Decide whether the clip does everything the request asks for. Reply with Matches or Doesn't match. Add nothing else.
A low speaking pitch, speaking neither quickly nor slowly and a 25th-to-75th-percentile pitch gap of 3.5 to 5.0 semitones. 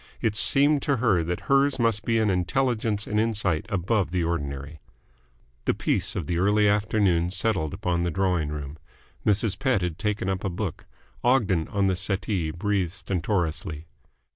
Matches